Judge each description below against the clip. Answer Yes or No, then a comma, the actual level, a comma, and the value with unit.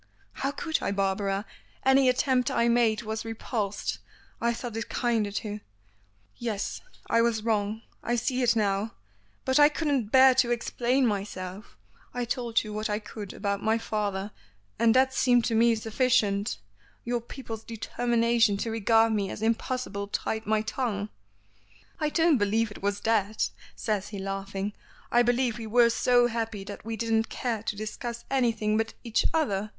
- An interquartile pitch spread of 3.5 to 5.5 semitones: No, narrow, 2.6 semitones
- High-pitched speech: Yes, high, 225 Hz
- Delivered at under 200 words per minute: Yes, average, 165 wpm